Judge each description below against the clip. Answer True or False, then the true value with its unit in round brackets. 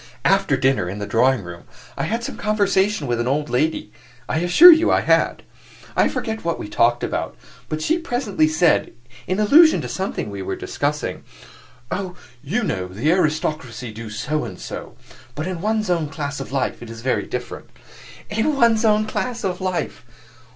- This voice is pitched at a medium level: True (160 Hz)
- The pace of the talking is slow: False (180 wpm)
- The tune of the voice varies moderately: False (9.0 semitones)